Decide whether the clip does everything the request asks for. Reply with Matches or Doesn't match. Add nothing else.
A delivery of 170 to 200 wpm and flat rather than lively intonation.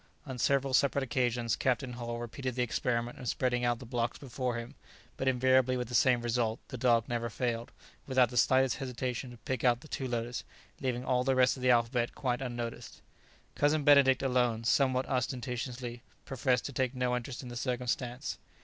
Matches